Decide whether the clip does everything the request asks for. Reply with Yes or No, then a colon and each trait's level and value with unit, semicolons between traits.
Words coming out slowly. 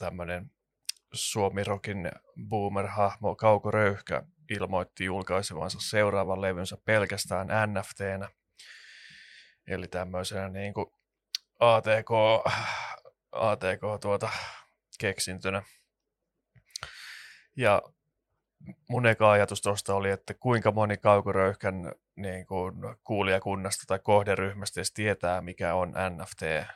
Yes: slow, 85 wpm